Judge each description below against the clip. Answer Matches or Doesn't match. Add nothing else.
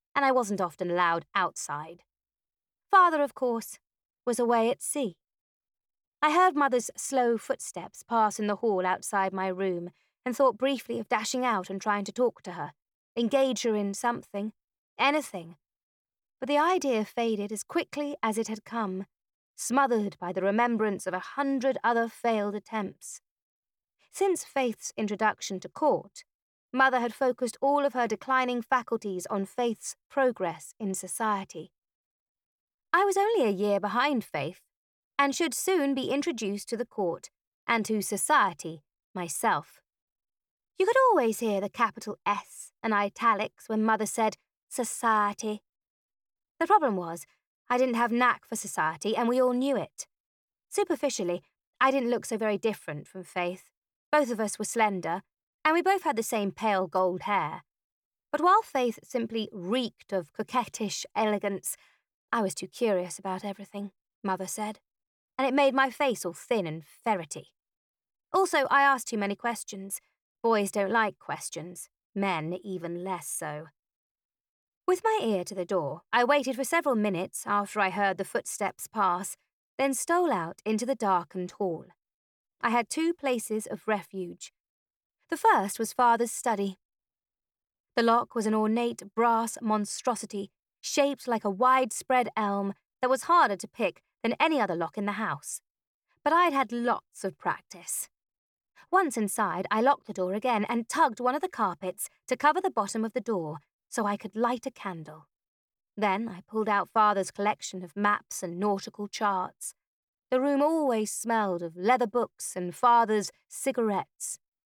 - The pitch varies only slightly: Doesn't match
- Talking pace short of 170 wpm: Matches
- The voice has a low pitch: Doesn't match